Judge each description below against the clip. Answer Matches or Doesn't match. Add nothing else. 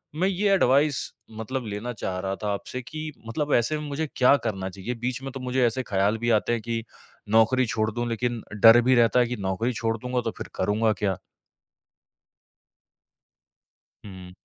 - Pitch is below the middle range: Matches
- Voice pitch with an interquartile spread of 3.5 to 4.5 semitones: Doesn't match